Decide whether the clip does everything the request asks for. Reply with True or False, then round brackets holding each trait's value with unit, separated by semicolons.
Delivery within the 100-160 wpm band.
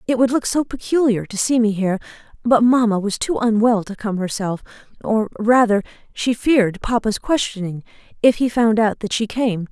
False (180 wpm)